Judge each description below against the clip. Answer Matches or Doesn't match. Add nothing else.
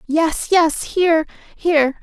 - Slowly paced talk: Matches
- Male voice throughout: Doesn't match